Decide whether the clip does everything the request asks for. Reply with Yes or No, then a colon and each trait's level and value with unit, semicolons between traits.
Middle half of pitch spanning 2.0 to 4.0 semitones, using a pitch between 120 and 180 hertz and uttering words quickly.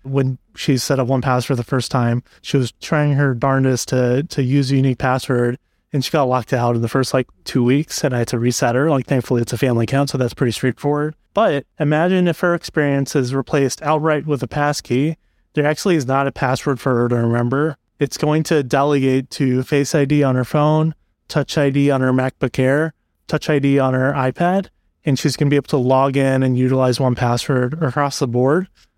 Yes: narrow, 2.5 semitones; low, 135 Hz; fast, 220 wpm